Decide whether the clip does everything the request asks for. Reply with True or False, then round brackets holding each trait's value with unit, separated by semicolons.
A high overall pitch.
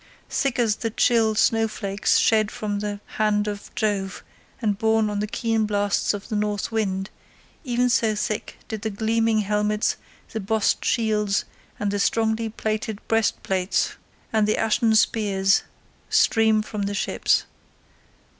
True (215 Hz)